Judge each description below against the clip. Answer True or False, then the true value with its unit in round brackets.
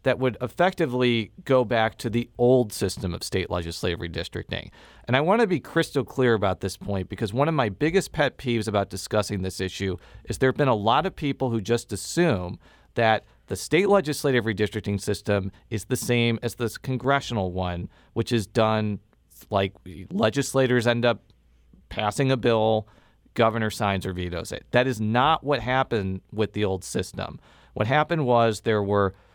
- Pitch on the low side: True (110 Hz)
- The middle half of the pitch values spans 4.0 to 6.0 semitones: True (4.4 semitones)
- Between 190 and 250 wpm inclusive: False (180 wpm)